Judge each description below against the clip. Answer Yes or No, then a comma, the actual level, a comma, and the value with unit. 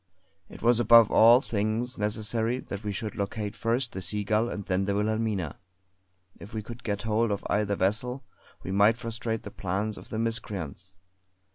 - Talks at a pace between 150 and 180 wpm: Yes, average, 170 wpm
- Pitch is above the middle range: No, low, 110 Hz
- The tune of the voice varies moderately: No, narrow, 2.2 semitones